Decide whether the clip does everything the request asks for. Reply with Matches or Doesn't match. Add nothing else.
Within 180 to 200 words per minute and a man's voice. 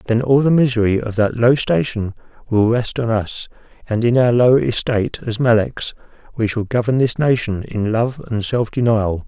Matches